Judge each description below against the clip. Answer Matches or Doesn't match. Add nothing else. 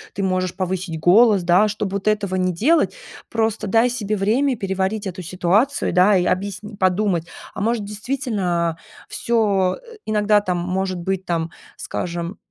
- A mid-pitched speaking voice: Doesn't match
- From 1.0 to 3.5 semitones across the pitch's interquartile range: Matches